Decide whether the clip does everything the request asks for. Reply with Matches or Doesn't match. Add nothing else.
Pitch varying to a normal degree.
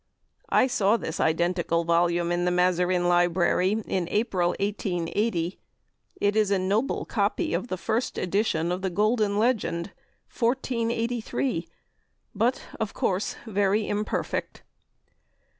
Matches